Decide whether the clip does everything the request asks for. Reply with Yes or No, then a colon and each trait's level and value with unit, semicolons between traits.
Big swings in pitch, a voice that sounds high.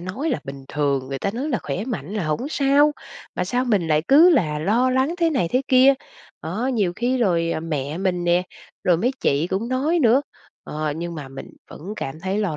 Yes: wide, 8.2 semitones; high, 195 Hz